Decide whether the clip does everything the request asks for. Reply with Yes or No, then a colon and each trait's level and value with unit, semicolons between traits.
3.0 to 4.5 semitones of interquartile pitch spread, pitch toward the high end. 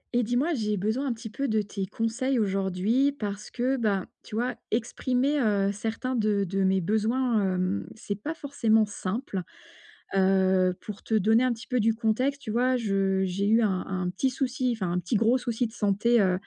Yes: average, 4.0 semitones; high, 220 Hz